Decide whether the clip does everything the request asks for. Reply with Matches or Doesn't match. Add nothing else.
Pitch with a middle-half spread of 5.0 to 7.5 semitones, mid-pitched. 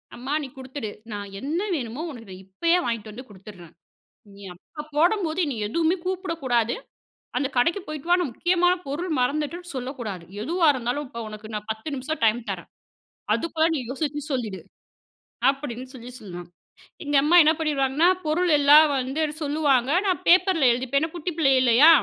Doesn't match